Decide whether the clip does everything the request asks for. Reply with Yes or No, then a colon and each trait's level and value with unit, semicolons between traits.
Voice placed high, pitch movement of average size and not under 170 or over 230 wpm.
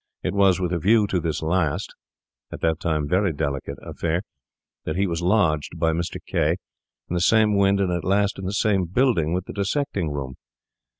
No: very low, 90 Hz; average, 3.6 semitones; average, 185 wpm